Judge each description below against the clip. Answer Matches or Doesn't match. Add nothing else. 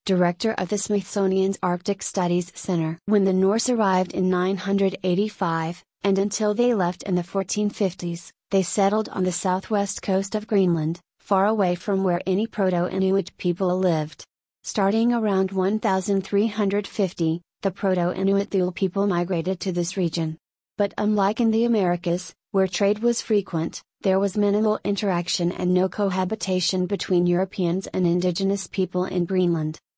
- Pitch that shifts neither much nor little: Doesn't match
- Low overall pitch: Doesn't match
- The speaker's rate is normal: Matches